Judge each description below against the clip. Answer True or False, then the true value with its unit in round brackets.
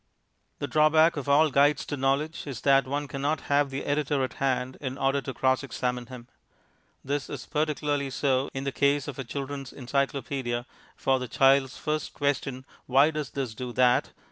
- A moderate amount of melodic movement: False (1.7 semitones)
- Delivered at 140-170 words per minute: False (180 wpm)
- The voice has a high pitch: False (140 Hz)